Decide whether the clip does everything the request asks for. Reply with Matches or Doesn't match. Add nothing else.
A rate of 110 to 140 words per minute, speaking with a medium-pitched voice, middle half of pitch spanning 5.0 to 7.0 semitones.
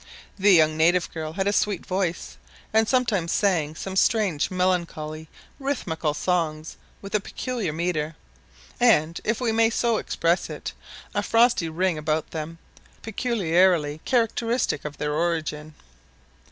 Matches